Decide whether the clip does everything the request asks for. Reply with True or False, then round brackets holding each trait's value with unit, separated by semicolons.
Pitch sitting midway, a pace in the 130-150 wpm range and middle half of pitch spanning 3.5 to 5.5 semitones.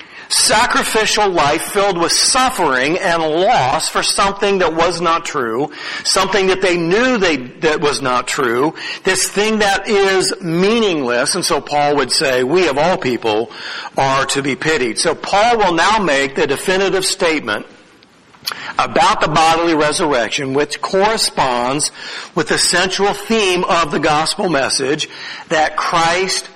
True (180 Hz; 145 wpm; 4.7 semitones)